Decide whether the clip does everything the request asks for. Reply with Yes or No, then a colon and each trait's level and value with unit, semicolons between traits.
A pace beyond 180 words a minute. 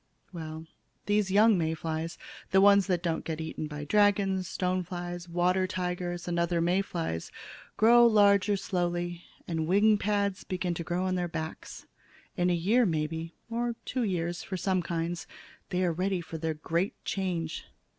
No: average, 165 wpm